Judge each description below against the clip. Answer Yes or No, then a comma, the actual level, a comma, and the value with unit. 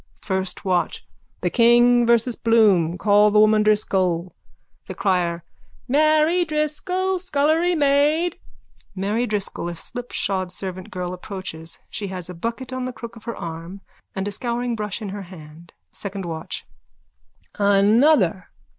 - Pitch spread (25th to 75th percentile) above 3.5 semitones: Yes, average, 5.0 semitones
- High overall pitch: Yes, high, 210 Hz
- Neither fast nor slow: No, slow, 130 wpm